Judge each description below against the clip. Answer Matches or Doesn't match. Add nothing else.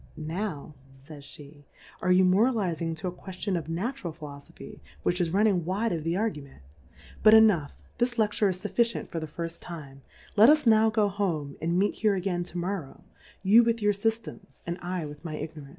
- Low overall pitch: Doesn't match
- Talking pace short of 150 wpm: Doesn't match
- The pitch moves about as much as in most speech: Matches